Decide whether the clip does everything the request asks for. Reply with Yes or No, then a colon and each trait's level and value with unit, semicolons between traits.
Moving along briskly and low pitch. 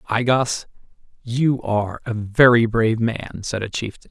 No: average, 160 wpm; low, 115 Hz